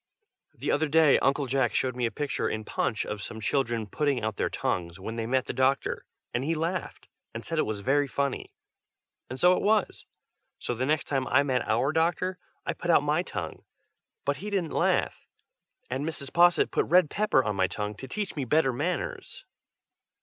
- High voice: No, low, 135 Hz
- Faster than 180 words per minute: Yes, average, 200 wpm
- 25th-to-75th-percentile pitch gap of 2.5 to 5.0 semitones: No, wide, 5.5 semitones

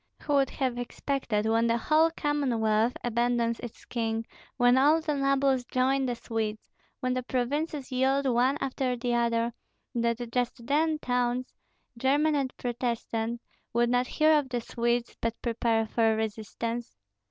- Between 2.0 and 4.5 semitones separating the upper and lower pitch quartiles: Yes, narrow, 2.6 semitones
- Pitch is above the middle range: Yes, high, 245 Hz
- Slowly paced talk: No, average, 150 wpm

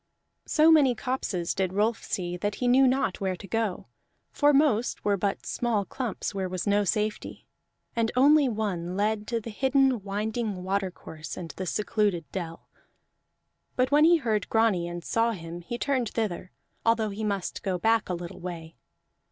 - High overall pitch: Yes, high, 210 Hz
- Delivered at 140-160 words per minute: No, average, 170 wpm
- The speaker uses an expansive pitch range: No, average, 4.4 semitones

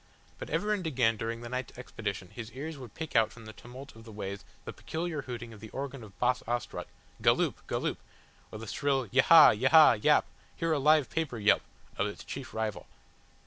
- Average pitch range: Yes, average, 4.2 semitones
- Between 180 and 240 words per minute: Yes, average, 200 wpm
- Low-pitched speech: Yes, low, 125 Hz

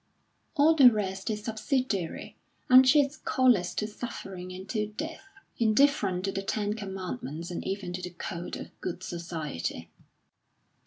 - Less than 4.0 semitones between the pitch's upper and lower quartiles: No, average, 5.3 semitones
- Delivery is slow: No, average, 150 wpm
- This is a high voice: Yes, high, 200 Hz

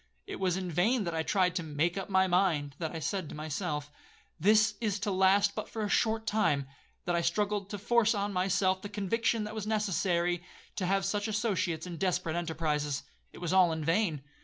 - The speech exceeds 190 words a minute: Yes, average, 200 wpm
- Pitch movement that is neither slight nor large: Yes, average, 3.8 semitones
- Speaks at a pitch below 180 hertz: No, medium, 185 Hz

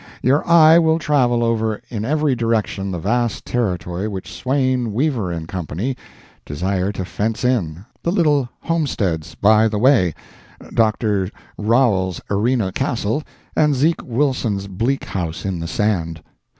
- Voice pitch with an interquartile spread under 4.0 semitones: No, wide, 5.4 semitones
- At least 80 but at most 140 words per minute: Yes, slow, 135 wpm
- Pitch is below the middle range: Yes, low, 110 Hz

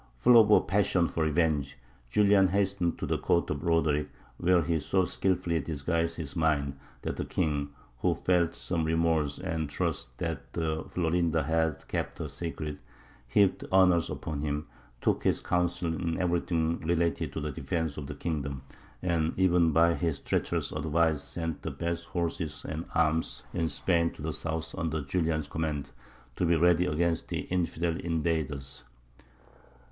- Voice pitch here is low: Yes, very low, 80 Hz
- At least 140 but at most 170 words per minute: Yes, average, 155 wpm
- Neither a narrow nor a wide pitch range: No, narrow, 2.0 semitones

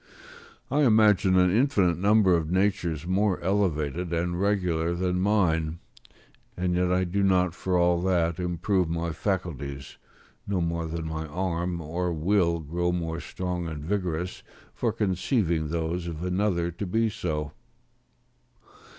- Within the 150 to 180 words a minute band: No, average, 140 wpm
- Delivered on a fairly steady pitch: Yes, narrow, 2.2 semitones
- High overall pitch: No, very low, 90 Hz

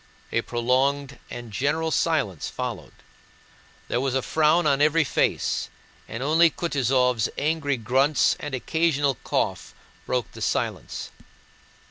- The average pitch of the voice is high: No, medium, 140 Hz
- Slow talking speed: Yes, slow, 120 wpm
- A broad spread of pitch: No, average, 3.6 semitones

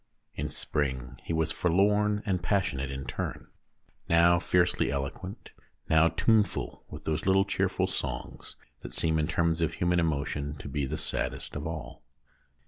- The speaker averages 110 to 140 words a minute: No, average, 150 wpm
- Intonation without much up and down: No, average, 3.7 semitones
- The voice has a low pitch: Yes, very low, 80 Hz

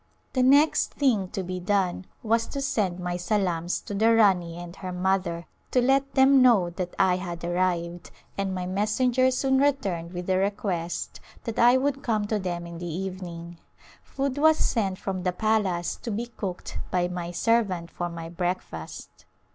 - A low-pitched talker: No, high, 190 Hz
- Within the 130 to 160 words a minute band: No, average, 175 wpm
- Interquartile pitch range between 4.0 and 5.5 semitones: Yes, average, 4.6 semitones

